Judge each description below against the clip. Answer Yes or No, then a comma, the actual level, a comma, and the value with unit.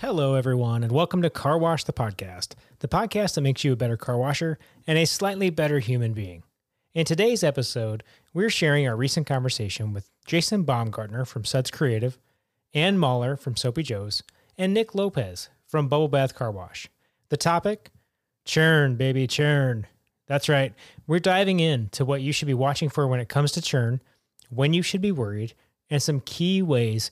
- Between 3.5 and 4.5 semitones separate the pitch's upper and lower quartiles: No, average, 5.2 semitones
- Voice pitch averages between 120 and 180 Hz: Yes, medium, 140 Hz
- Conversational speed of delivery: Yes, average, 180 wpm